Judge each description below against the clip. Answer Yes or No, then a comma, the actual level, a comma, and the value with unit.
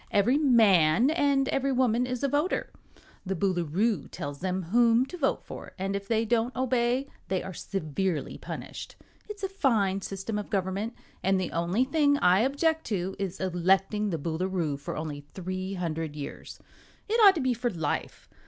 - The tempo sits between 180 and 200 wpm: No, average, 170 wpm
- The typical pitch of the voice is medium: No, high, 200 Hz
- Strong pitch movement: Yes, wide, 5.8 semitones